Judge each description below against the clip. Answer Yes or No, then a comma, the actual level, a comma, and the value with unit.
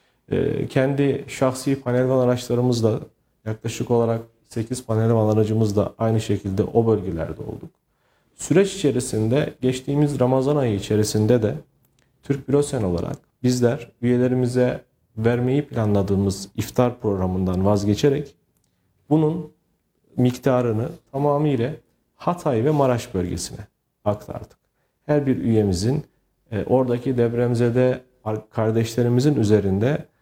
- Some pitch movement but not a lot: Yes, average, 3.8 semitones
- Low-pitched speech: Yes, low, 120 Hz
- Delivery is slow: Yes, slow, 90 wpm